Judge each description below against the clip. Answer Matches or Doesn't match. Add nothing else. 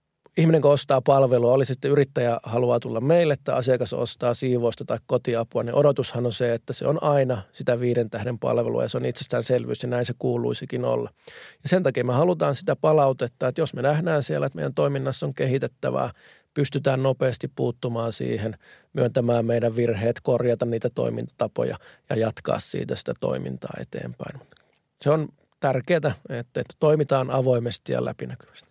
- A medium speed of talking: Doesn't match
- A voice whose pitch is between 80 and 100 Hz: Doesn't match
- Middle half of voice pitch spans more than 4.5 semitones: Doesn't match